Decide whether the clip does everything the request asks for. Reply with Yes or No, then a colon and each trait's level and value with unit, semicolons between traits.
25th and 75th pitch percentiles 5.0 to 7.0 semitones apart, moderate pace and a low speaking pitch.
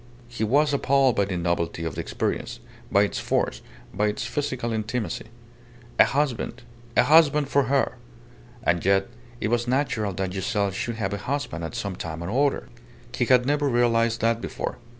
Yes: wide, 5.4 semitones; average, 175 wpm; low, 115 Hz